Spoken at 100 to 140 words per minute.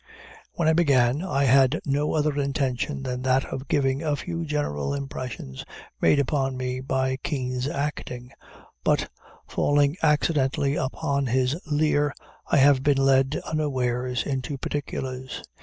Yes: slow, 135 wpm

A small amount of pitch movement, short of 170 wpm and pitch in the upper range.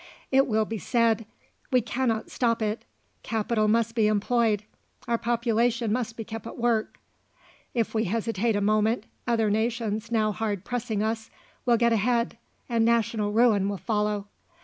Yes: narrow, 1.6 semitones; average, 155 wpm; high, 225 Hz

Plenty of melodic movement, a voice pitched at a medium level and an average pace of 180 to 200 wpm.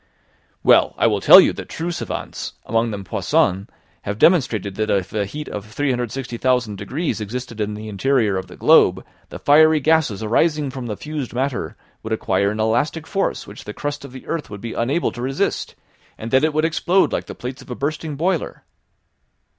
No: wide, 5.9 semitones; low, 125 Hz; average, 195 wpm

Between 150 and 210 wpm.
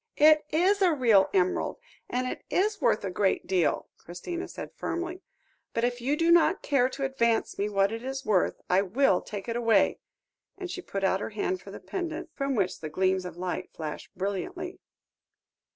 Yes: average, 190 wpm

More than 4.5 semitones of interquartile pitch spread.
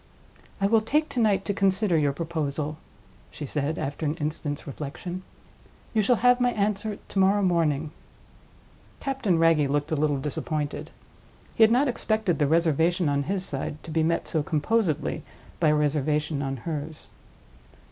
Yes: average, 5.2 semitones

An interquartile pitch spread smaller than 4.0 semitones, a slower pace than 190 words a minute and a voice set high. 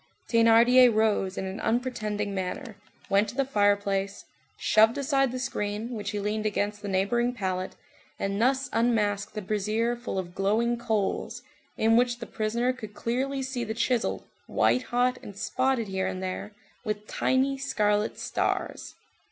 Yes: average, 3.2 semitones; average, 155 wpm; high, 220 Hz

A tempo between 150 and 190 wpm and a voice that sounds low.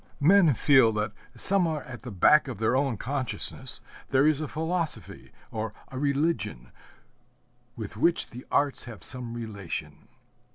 No: average, 140 wpm; low, 130 Hz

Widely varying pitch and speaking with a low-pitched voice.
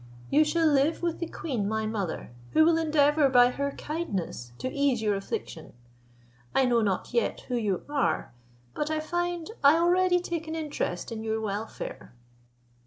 No: wide, 6.6 semitones; very high, 280 Hz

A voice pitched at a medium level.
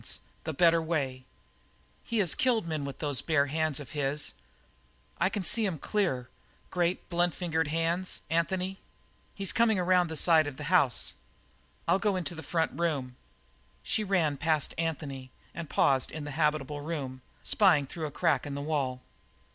Yes: medium, 160 Hz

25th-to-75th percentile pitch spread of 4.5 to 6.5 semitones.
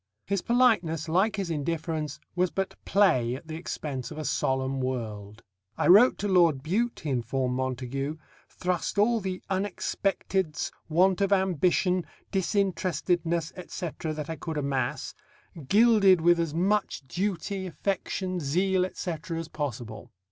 Yes: average, 4.8 semitones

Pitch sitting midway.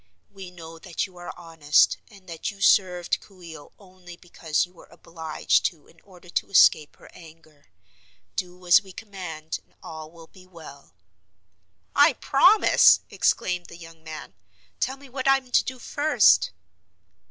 Yes: medium, 175 Hz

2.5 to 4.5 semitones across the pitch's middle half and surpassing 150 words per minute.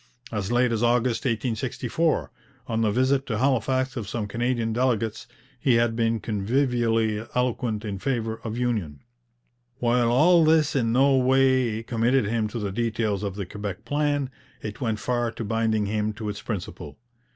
Yes: average, 2.8 semitones; average, 165 wpm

